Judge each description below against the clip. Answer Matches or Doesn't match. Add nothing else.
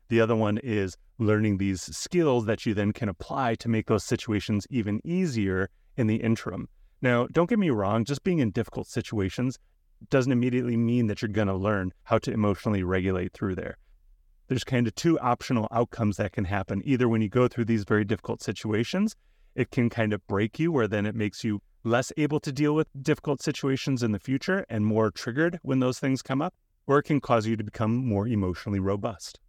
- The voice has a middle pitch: Doesn't match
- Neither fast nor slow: Doesn't match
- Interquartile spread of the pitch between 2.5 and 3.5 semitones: Doesn't match